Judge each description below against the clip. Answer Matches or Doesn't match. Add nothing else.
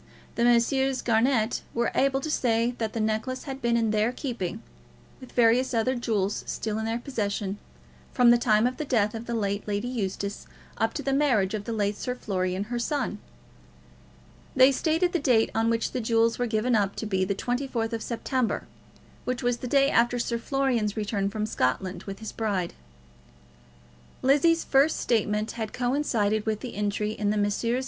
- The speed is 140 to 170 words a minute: Doesn't match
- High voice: Matches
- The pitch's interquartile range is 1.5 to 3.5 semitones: Matches